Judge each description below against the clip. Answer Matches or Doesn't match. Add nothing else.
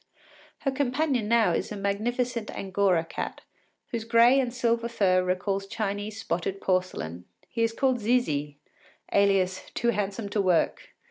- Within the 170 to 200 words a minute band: Doesn't match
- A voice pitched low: Doesn't match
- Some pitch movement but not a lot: Matches